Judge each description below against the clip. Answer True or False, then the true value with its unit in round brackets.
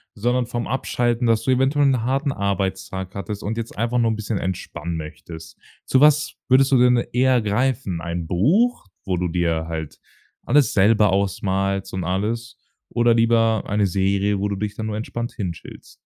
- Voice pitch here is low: True (110 Hz)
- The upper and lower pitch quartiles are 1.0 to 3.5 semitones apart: False (4.3 semitones)